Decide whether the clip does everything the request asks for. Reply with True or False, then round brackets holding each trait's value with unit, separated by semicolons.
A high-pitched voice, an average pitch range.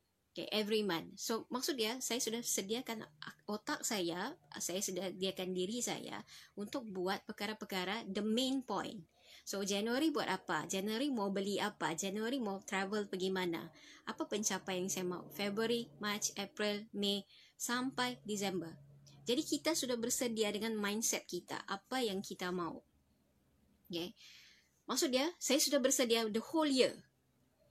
True (205 Hz; 4.0 semitones)